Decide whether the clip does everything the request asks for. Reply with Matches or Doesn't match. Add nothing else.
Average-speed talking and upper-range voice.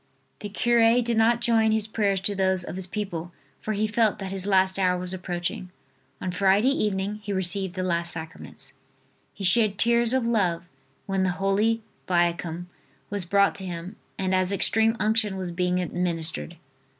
Matches